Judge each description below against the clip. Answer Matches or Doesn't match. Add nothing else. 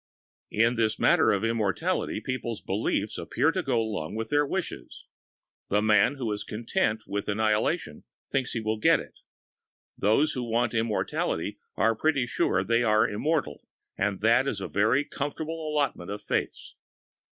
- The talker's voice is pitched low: Matches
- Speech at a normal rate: Matches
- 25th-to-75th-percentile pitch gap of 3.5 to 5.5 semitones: Matches